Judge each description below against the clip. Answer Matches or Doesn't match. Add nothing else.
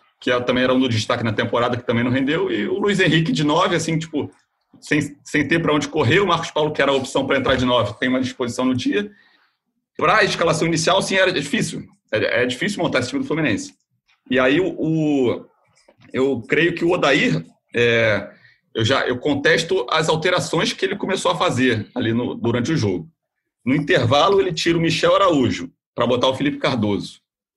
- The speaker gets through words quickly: Matches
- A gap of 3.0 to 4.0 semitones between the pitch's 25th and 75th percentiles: Doesn't match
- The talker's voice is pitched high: Doesn't match